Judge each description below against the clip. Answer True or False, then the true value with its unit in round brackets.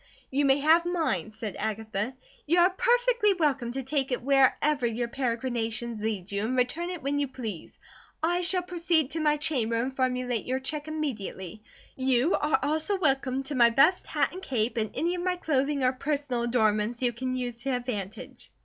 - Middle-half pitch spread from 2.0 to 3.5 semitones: False (4.7 semitones)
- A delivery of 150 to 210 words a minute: True (185 wpm)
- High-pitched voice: True (265 Hz)